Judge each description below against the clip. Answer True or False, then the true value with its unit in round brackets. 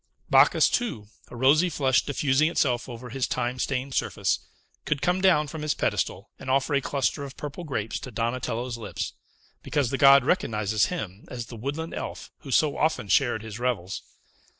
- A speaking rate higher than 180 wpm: False (175 wpm)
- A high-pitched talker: False (130 Hz)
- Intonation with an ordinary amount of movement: True (3.9 semitones)